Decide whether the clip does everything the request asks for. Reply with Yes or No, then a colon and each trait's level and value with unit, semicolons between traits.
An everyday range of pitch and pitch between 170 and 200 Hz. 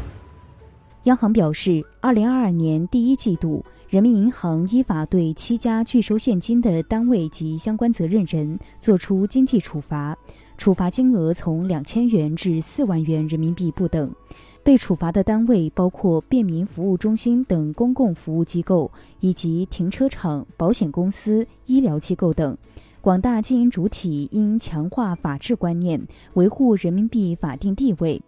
No: wide, 5.8 semitones; medium, 185 Hz